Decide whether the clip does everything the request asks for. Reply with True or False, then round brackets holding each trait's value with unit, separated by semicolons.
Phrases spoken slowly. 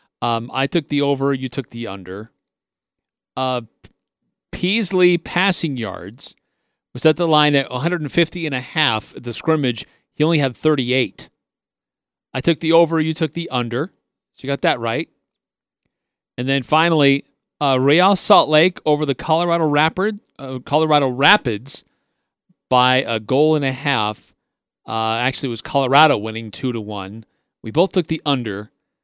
False (155 wpm)